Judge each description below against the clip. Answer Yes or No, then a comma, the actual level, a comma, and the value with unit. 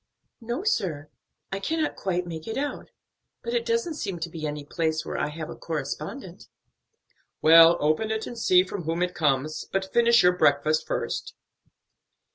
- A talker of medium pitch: Yes, medium, 175 Hz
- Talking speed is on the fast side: No, average, 170 wpm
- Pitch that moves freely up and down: Yes, wide, 6.1 semitones